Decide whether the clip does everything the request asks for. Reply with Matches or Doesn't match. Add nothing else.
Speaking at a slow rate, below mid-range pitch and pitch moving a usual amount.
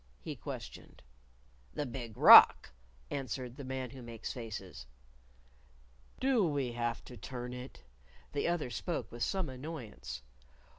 Matches